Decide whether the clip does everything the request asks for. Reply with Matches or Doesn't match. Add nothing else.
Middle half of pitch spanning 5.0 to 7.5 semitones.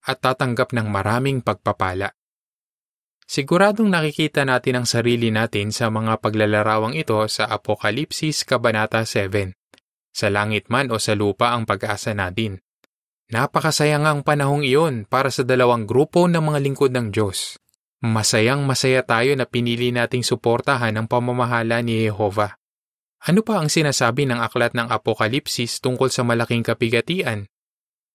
Doesn't match